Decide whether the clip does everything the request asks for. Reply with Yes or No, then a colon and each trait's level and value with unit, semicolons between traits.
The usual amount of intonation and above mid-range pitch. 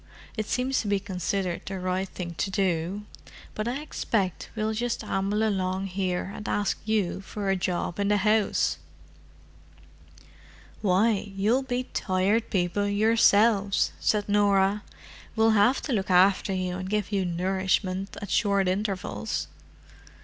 No: narrow, 2.3 semitones; high, 200 Hz